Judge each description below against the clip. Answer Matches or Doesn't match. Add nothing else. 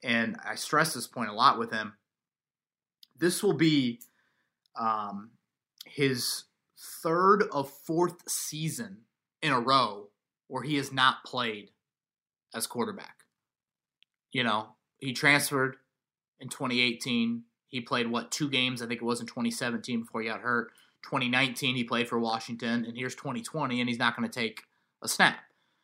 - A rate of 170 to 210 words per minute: Doesn't match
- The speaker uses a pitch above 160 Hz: Doesn't match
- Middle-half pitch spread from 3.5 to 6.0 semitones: Doesn't match